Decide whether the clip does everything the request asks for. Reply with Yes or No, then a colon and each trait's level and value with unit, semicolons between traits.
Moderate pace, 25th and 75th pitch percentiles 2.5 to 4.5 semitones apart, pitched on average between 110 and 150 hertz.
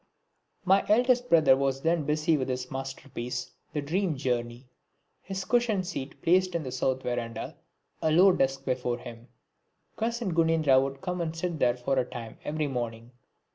No: average, 165 wpm; wide, 5.4 semitones; medium, 140 Hz